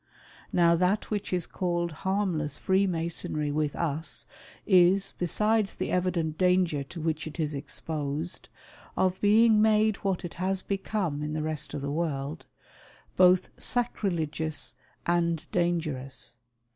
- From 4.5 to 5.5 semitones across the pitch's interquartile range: No, average, 3.5 semitones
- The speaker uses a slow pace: Yes, slow, 130 wpm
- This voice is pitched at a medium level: Yes, medium, 170 Hz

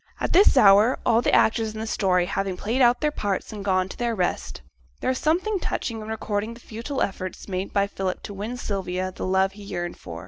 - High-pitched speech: Yes, high, 205 Hz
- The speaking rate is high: Yes, fast, 235 wpm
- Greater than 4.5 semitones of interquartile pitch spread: No, average, 3.7 semitones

